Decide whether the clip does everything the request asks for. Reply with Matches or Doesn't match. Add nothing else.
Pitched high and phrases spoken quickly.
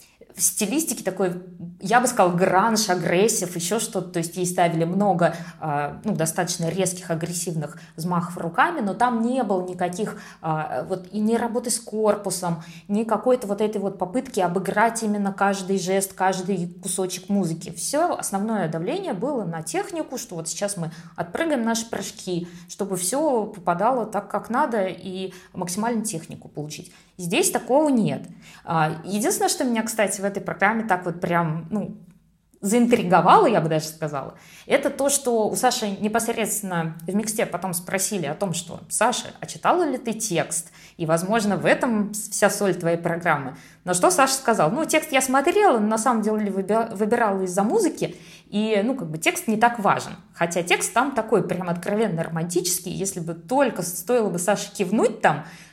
Matches